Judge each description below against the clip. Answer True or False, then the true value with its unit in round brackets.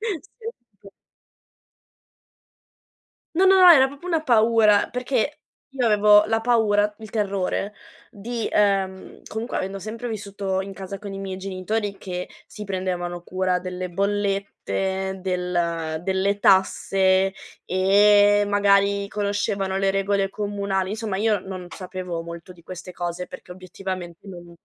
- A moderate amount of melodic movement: False (2.0 semitones)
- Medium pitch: False (195 Hz)